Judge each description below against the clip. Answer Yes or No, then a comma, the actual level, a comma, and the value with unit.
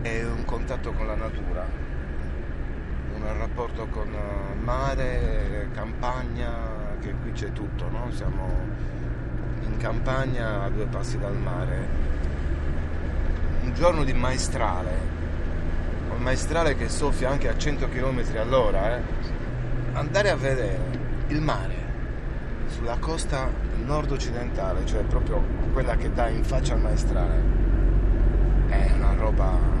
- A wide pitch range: Yes, wide, 9.0 semitones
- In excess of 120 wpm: No, slow, 115 wpm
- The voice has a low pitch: Yes, very low, 80 Hz